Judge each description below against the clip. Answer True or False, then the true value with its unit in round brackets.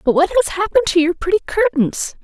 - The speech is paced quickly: True (215 wpm)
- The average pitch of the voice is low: False (370 Hz)